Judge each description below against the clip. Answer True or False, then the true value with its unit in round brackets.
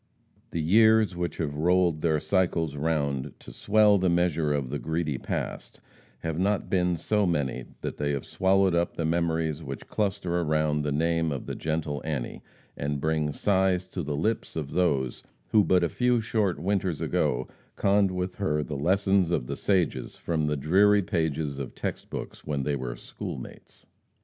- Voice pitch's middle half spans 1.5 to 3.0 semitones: False (4.1 semitones)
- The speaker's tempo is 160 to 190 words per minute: True (175 wpm)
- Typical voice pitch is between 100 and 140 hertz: False (80 Hz)